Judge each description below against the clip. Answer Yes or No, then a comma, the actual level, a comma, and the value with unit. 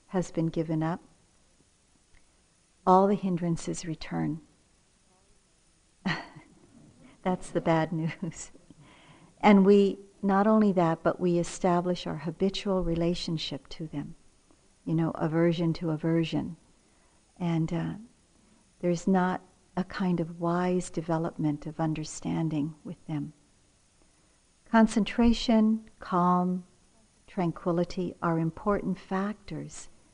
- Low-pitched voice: No, medium, 175 Hz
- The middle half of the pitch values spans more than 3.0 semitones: No, narrow, 2.6 semitones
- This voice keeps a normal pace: No, slow, 100 wpm